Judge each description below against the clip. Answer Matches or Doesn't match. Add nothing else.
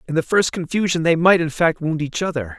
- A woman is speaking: Doesn't match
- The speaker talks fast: Matches